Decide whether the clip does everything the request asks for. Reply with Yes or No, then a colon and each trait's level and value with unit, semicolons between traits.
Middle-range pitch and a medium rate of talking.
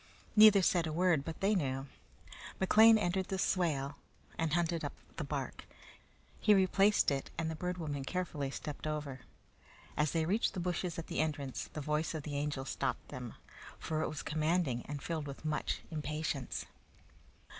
Yes: medium, 155 Hz; average, 170 wpm